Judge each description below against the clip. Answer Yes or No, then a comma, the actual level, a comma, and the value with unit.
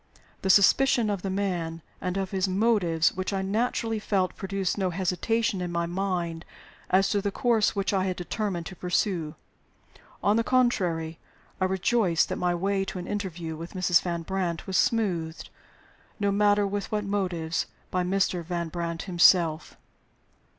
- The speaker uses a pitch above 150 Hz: Yes, high, 190 Hz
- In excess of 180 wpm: No, average, 165 wpm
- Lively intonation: No, average, 2.7 semitones